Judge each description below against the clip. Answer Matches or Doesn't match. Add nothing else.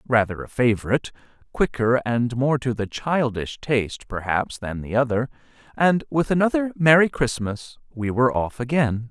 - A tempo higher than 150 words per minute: Doesn't match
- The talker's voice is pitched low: Matches